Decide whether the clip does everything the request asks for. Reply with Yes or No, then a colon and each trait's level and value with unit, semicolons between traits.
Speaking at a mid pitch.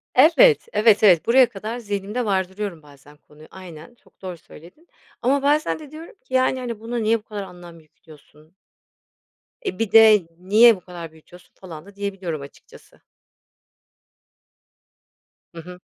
No: high, 200 Hz